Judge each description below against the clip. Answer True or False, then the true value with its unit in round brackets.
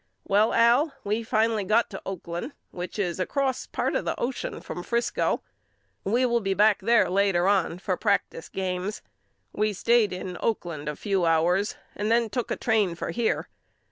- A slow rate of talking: False (170 wpm)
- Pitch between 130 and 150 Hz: False (205 Hz)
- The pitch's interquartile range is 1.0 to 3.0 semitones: False (4.1 semitones)